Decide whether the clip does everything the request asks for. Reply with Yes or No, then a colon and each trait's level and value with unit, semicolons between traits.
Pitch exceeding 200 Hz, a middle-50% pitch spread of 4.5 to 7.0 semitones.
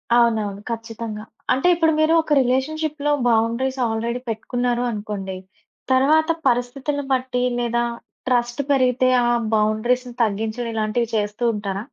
No: high, 240 Hz; average, 3.0 semitones